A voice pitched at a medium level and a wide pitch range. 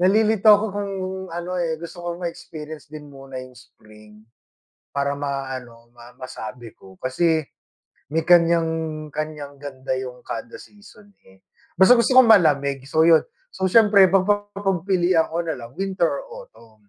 Yes: medium, 160 Hz; wide, 6.0 semitones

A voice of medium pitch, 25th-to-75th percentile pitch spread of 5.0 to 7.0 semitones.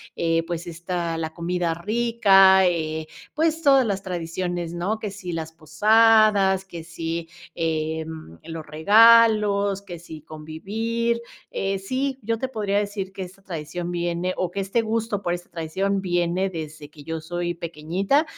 No: medium, 180 Hz; average, 3.8 semitones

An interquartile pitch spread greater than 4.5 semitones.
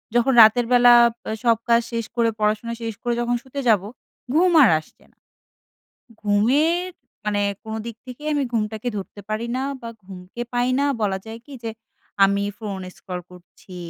No: average, 2.9 semitones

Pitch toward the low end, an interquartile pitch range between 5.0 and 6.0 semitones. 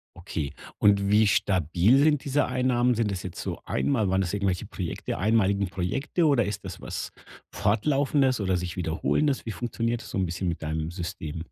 Yes: low, 100 Hz; wide, 5.4 semitones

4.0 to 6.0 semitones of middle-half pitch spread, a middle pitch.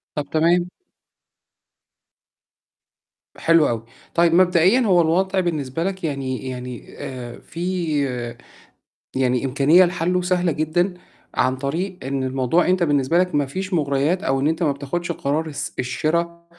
Yes: average, 4.4 semitones; medium, 160 Hz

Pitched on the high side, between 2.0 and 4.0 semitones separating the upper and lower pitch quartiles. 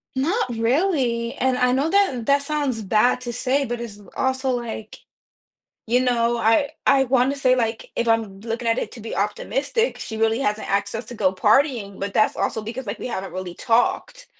Yes: high, 240 Hz; average, 3.1 semitones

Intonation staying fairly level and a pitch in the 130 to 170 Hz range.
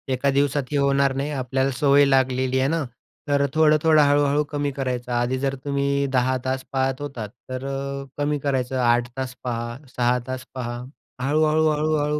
Yes: narrow, 2.0 semitones; low, 135 Hz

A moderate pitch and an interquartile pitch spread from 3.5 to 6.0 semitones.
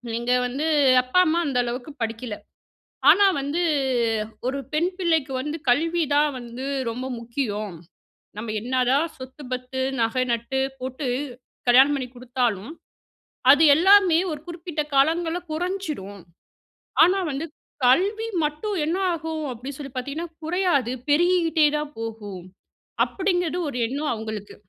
No: very high, 280 Hz; average, 5.1 semitones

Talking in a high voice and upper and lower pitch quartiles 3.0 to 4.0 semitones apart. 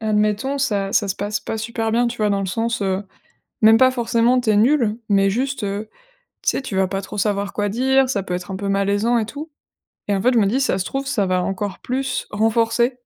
Yes: high, 215 Hz; average, 3.4 semitones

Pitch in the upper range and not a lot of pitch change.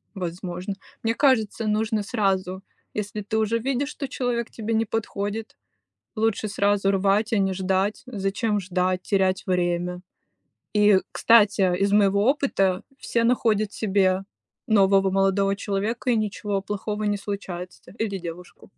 Yes: high, 200 Hz; narrow, 2.3 semitones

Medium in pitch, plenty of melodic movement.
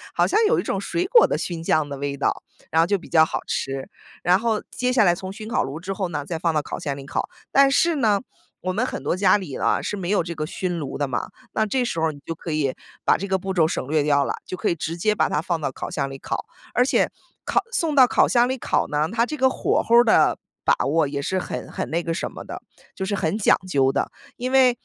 Yes: medium, 180 Hz; wide, 6.6 semitones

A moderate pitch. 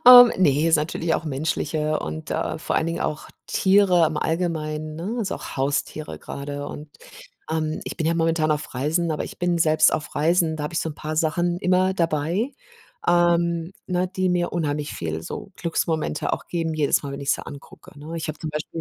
Yes: medium, 160 Hz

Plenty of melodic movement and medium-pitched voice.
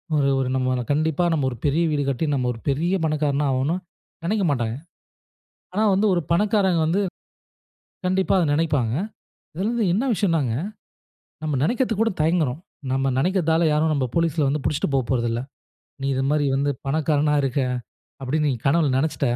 No: average, 4.0 semitones; medium, 150 Hz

